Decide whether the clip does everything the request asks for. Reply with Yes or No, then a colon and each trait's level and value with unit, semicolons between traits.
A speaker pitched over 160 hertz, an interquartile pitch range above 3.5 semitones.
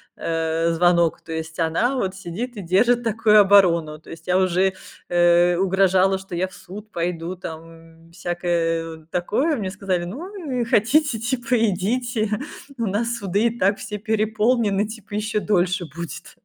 Yes: high, 190 Hz; average, 4.3 semitones